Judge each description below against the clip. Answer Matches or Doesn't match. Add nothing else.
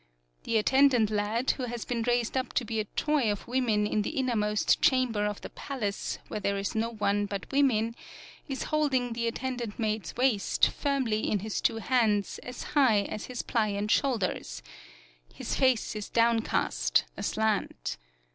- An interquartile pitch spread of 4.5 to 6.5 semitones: Doesn't match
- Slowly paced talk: Doesn't match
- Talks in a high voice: Matches